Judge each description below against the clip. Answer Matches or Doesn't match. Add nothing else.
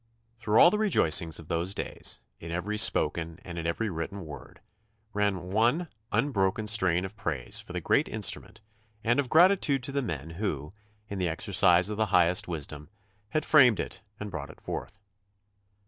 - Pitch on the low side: Matches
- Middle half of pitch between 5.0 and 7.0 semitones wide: Matches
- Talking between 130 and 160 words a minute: Doesn't match